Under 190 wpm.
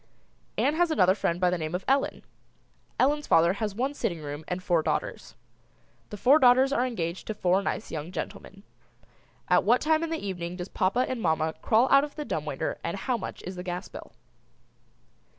No: average, 200 wpm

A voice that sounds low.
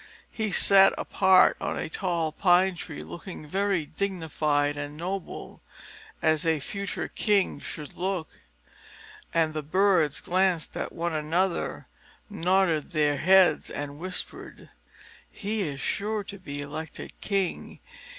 No: medium, 175 Hz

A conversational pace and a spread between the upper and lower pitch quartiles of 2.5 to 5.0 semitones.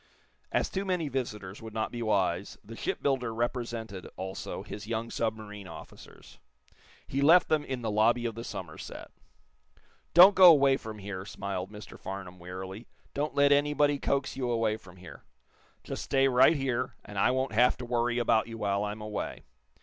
Yes: average, 170 wpm; average, 4.5 semitones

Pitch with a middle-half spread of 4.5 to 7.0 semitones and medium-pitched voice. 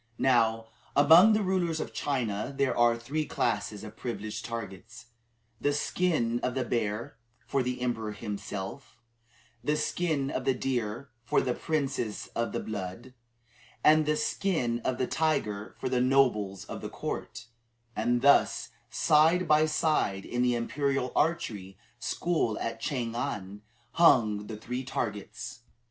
No: average, 4.8 semitones; low, 125 Hz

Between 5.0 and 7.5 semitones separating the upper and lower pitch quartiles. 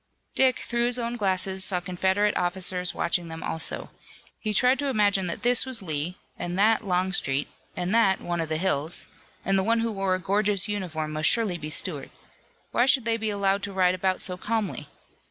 No: average, 3.6 semitones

